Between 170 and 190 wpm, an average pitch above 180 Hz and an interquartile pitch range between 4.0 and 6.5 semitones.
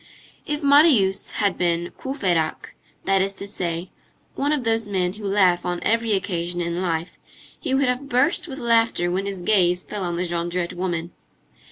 Yes: average, 175 wpm; high, 190 Hz; average, 4.7 semitones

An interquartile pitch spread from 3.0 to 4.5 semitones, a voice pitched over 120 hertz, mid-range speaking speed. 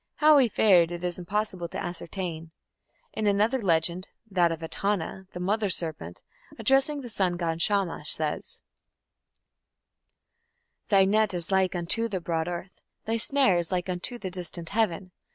Yes: average, 3.7 semitones; medium, 185 Hz; average, 155 wpm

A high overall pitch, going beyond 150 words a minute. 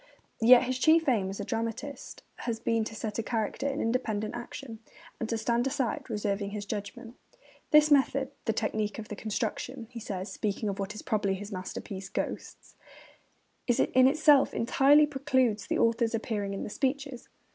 Yes: high, 230 Hz; average, 170 wpm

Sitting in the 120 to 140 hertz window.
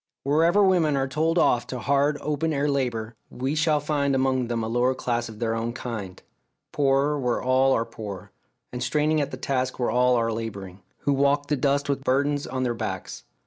Yes: low, 135 Hz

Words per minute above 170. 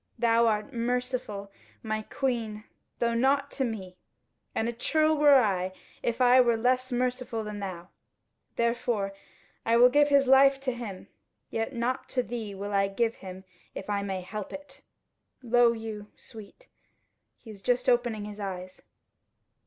No: average, 155 wpm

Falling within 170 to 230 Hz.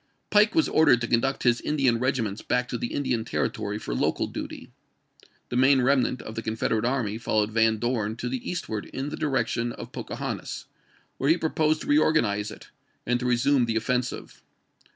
No: low, 125 Hz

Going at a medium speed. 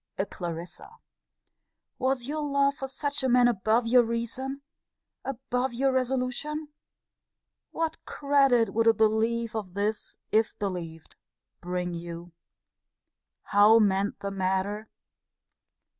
No: slow, 115 wpm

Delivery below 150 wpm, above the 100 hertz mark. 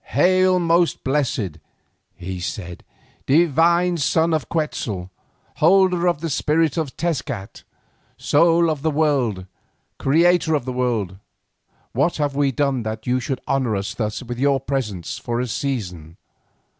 Yes: average, 140 wpm; medium, 140 Hz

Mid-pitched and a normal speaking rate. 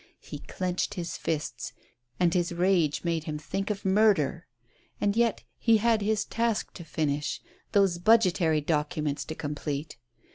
Yes: medium, 175 Hz; average, 150 wpm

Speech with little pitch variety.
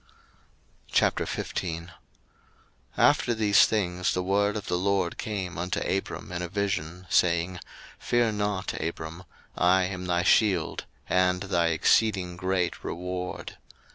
Yes: narrow, 2.0 semitones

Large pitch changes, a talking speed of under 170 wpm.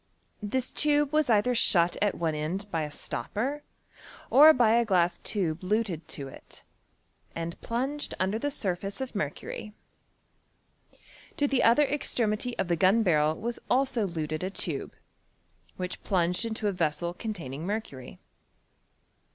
Yes: wide, 5.9 semitones; average, 145 wpm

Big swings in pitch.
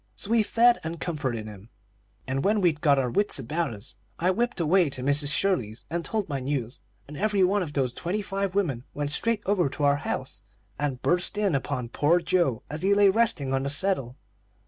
Yes: wide, 6.3 semitones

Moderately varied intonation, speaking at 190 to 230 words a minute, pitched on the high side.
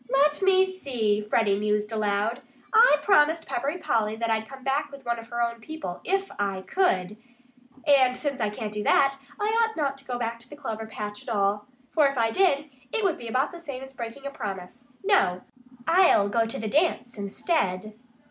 No: wide, 5.7 semitones; fast, 205 wpm; high, 245 Hz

